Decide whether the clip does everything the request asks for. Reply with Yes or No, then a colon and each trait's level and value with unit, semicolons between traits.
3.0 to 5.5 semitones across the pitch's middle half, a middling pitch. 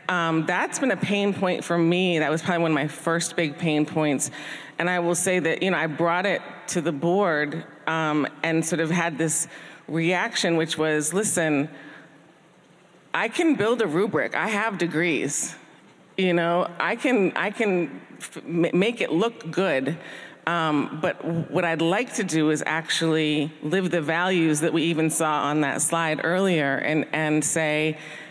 No: narrow, 2.4 semitones; medium, 165 Hz